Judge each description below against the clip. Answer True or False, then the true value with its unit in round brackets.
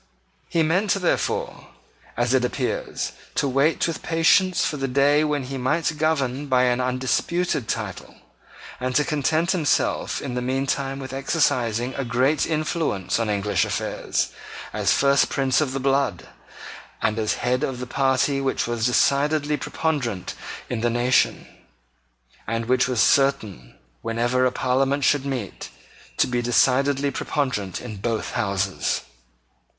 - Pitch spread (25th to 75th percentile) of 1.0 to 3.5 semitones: True (3.0 semitones)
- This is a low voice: True (130 Hz)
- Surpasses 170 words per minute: False (145 wpm)